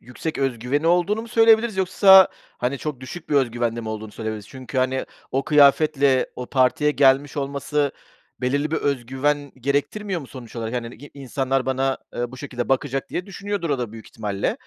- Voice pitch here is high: No, low, 135 Hz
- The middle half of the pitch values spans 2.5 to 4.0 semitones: Yes, average, 3.2 semitones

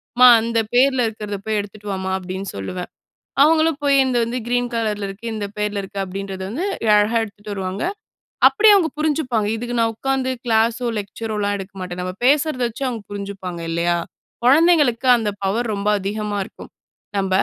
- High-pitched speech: Yes, high, 215 Hz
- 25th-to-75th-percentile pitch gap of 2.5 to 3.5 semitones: No, average, 4.0 semitones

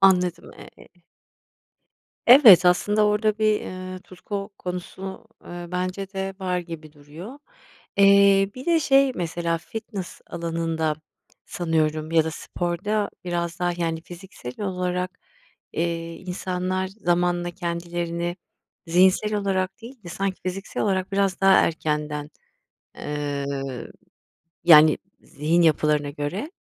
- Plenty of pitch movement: No, average, 2.8 semitones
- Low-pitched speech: No, medium, 180 Hz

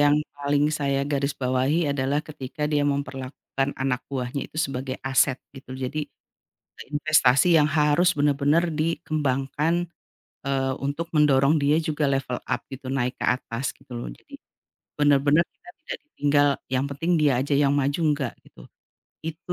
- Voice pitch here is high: No, medium, 140 Hz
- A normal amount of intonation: No, narrow, 1.9 semitones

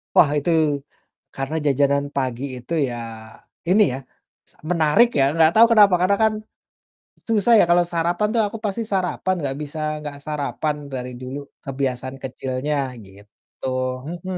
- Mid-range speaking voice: Yes, medium, 150 Hz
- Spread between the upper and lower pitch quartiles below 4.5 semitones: No, average, 5.3 semitones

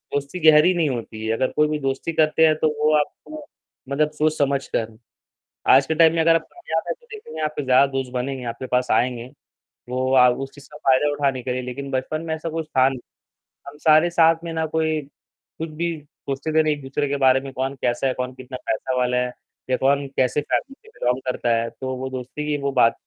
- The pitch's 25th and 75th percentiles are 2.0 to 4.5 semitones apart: Yes, average, 3.4 semitones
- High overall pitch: No, medium, 140 Hz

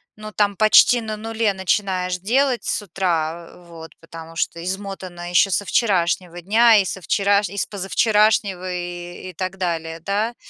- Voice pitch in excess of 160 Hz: Yes, high, 190 Hz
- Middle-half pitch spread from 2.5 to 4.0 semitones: Yes, average, 3.1 semitones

